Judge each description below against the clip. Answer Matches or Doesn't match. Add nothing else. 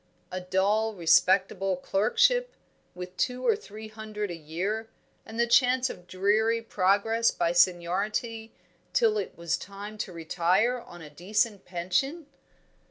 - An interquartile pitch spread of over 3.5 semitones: Matches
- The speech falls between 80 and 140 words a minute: Matches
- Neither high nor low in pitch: Doesn't match